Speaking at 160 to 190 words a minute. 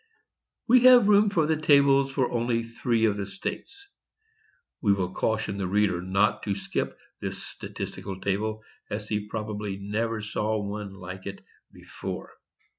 No: average, 150 wpm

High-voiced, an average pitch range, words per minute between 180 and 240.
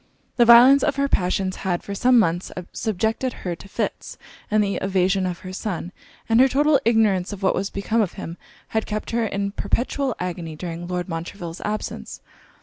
Yes: high, 200 Hz; average, 4.1 semitones; average, 185 wpm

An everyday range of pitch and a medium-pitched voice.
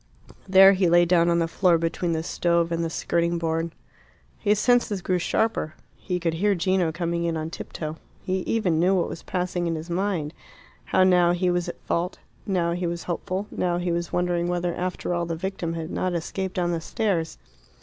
No: narrow, 1.6 semitones; medium, 175 Hz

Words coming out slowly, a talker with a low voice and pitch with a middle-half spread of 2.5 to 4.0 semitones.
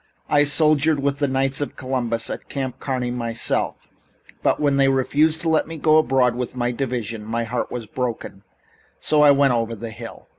No: average, 190 wpm; low, 130 Hz; average, 3.4 semitones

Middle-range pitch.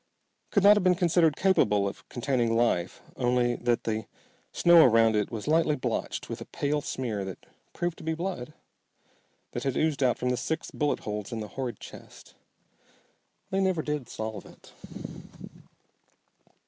No: low, 130 Hz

